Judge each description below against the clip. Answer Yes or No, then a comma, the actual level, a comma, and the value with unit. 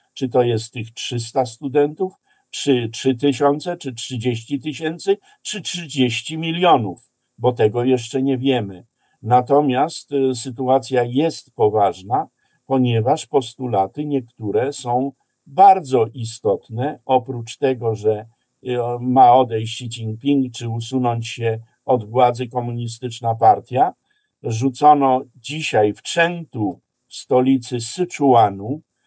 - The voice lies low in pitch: Yes, low, 130 Hz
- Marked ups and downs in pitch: No, average, 3.3 semitones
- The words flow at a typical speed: No, slow, 105 wpm